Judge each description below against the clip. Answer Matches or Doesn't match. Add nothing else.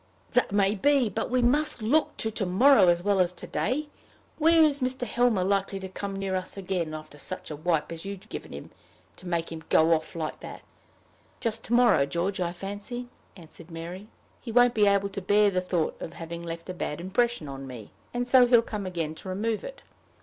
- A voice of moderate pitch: Doesn't match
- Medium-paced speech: Doesn't match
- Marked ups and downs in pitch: Matches